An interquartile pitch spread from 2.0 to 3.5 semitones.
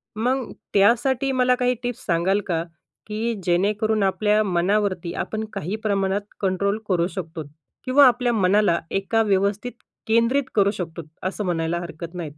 No: average, 3.9 semitones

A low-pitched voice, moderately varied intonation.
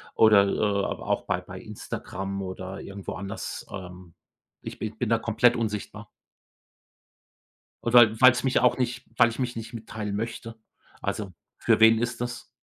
Yes: low, 110 Hz; average, 3.1 semitones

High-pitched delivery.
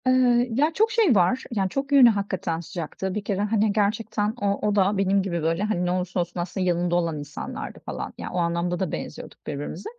Yes: high, 195 Hz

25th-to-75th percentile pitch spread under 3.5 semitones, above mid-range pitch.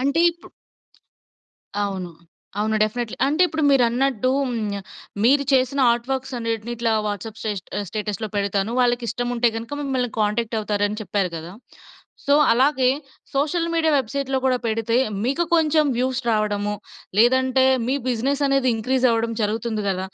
No: average, 3.8 semitones; high, 240 Hz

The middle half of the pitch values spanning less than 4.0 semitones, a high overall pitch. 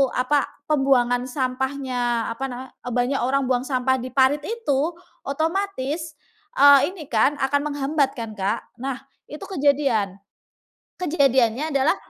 Yes: narrow, 2.6 semitones; very high, 270 Hz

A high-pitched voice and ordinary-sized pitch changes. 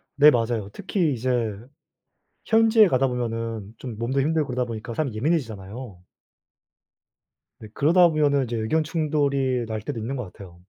No: low, 125 Hz; average, 5.0 semitones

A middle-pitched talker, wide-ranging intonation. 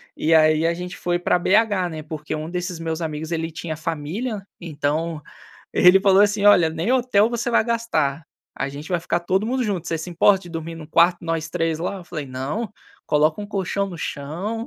No: medium, 170 Hz; average, 4.0 semitones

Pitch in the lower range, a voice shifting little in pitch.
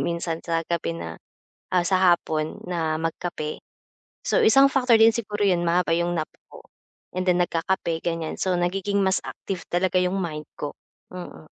No: medium, 175 Hz; narrow, 2.3 semitones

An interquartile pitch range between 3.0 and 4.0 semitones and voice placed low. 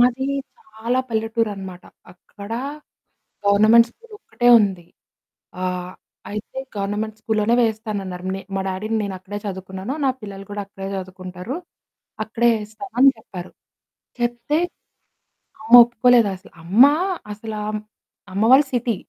No: average, 3.4 semitones; high, 215 Hz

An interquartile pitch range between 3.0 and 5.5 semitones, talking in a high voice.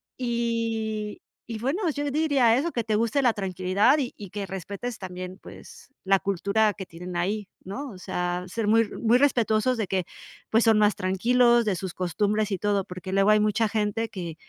Yes: average, 3.5 semitones; high, 210 Hz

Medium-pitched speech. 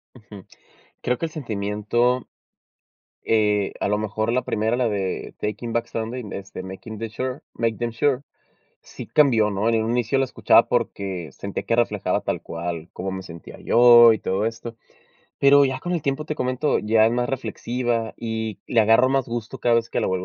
No: low, 115 Hz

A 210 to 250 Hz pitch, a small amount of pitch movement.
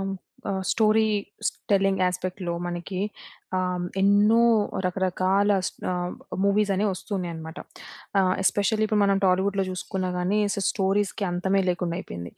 No: high, 190 Hz; narrow, 1.9 semitones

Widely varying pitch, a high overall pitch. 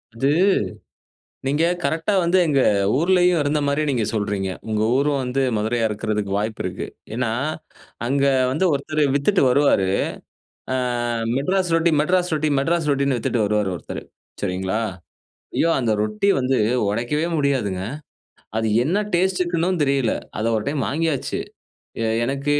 No: wide, 6.4 semitones; medium, 140 Hz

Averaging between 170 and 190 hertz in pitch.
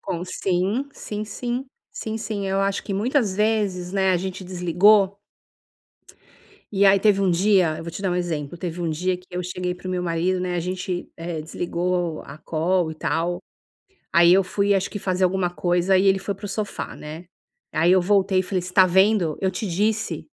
Yes: medium, 185 Hz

